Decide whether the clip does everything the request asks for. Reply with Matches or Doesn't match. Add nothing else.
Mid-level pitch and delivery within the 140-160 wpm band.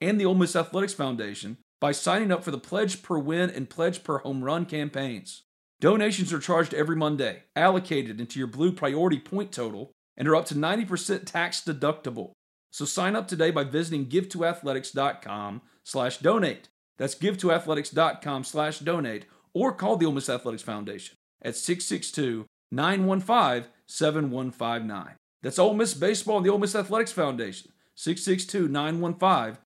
Matches